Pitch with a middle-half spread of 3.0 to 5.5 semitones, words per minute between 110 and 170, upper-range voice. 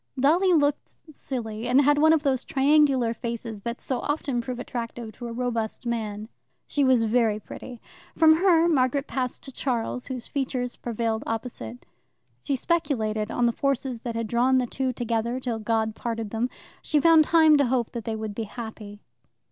No: average, 3.4 semitones; average, 180 wpm; high, 245 Hz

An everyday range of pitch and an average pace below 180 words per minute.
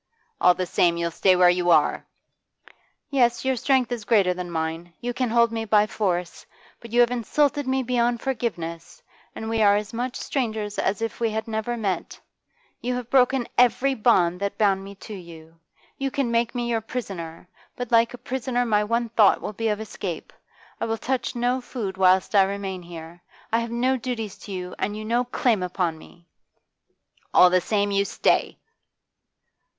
No: average, 4.5 semitones; average, 185 wpm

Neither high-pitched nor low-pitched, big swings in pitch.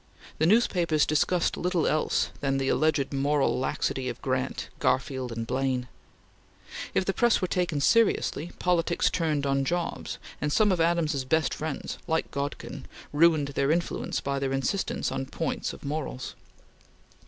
No: medium, 150 Hz; average, 3.9 semitones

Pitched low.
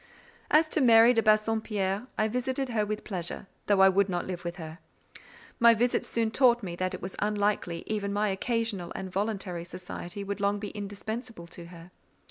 No: high, 205 Hz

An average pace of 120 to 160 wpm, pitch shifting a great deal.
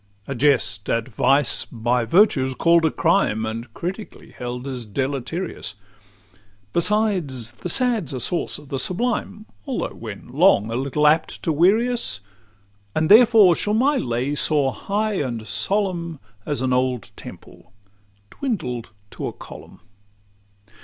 Yes: average, 140 wpm; wide, 7.8 semitones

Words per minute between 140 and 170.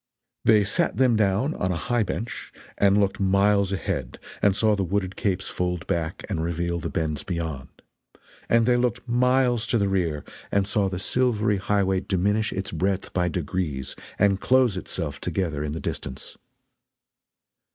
Yes: average, 160 wpm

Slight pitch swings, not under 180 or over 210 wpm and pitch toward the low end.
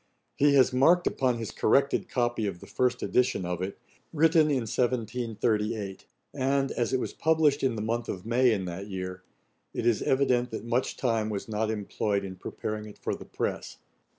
No: average, 3.7 semitones; average, 185 wpm; low, 115 Hz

